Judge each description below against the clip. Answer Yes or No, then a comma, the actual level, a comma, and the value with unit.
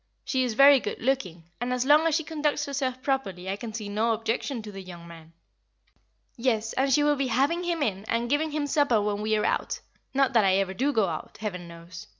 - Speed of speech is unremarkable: No, fast, 230 wpm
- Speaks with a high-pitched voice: Yes, high, 235 Hz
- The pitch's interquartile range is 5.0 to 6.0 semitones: Yes, wide, 5.4 semitones